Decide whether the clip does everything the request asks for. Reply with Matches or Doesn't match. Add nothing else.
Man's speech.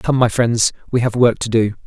Matches